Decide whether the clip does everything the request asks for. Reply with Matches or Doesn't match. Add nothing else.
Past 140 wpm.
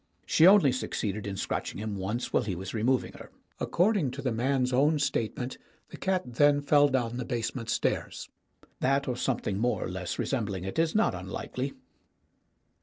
Matches